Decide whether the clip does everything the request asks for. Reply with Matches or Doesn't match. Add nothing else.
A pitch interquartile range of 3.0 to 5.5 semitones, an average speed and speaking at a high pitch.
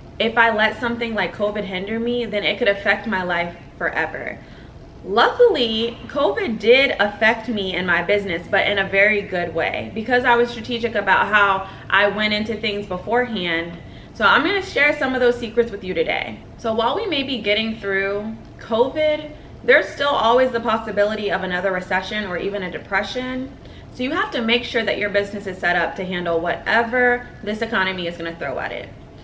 Matches